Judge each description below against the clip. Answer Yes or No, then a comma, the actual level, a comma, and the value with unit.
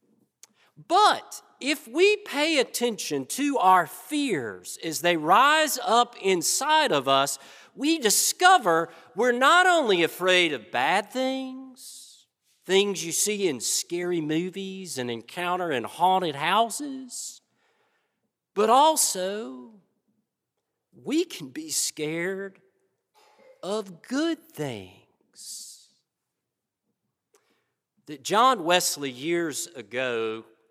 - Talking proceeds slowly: Yes, slow, 95 wpm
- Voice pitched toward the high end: Yes, high, 205 Hz